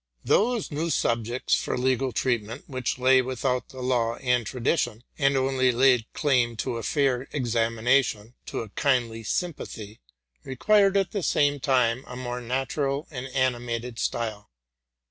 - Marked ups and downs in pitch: No, narrow, 2.5 semitones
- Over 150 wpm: No, average, 145 wpm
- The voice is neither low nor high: No, low, 125 Hz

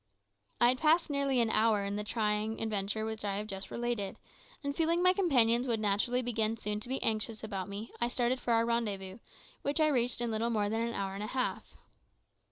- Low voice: No, high, 225 Hz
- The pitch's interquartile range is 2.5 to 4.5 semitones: Yes, average, 2.8 semitones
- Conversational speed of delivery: No, fast, 220 wpm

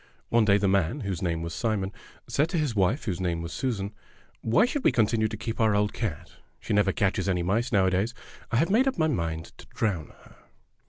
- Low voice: Yes, low, 105 Hz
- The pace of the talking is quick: Yes, fast, 220 wpm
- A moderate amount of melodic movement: Yes, average, 4.0 semitones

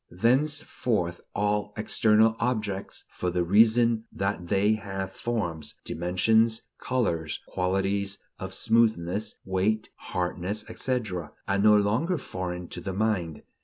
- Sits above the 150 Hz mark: No, low, 100 Hz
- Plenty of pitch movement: No, average, 3.5 semitones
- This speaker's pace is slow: Yes, slow, 115 wpm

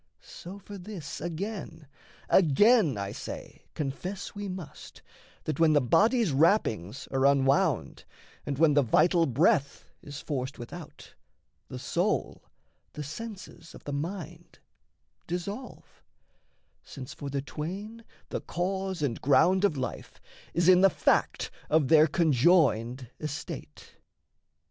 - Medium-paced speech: No, slow, 125 wpm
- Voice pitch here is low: No, medium, 160 Hz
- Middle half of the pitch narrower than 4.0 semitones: No, average, 5.3 semitones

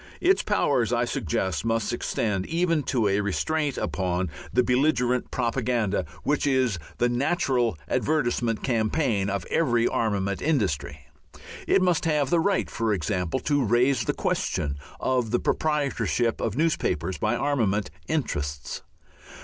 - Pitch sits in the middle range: No, low, 120 Hz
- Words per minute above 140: No, slow, 135 wpm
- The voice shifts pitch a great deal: Yes, wide, 6.2 semitones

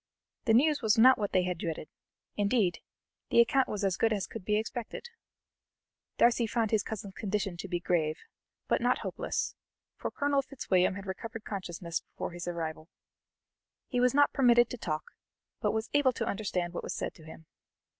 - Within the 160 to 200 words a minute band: Yes, average, 180 wpm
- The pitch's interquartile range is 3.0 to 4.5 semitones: No, average, 5.1 semitones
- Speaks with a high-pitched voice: Yes, high, 210 Hz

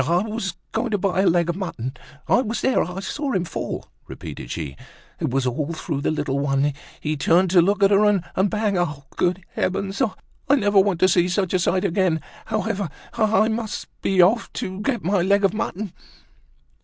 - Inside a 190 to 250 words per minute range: Yes, average, 200 wpm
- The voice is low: No, high, 190 Hz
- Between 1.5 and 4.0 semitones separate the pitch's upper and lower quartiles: Yes, average, 3.5 semitones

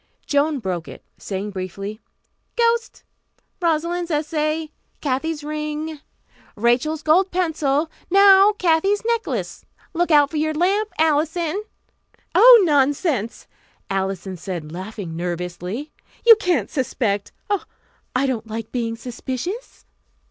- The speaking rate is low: Yes, slow, 110 wpm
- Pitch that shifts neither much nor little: No, wide, 7.7 semitones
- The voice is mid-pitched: No, very high, 300 Hz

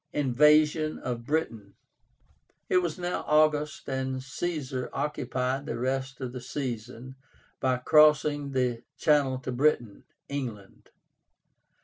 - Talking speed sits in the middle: No, slow, 110 wpm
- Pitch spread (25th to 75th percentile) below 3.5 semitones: Yes, average, 3.1 semitones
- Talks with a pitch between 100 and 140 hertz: Yes, low, 135 Hz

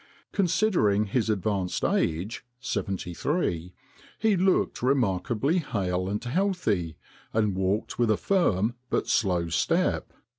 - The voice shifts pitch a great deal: Yes, wide, 7.5 semitones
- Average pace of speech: No, slow, 115 wpm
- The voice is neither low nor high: No, low, 105 Hz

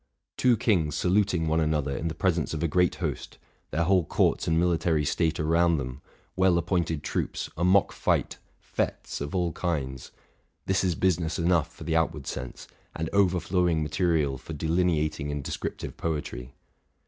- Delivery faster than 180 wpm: No, average, 165 wpm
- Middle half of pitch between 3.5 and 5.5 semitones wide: No, average, 2.7 semitones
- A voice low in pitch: Yes, very low, 80 Hz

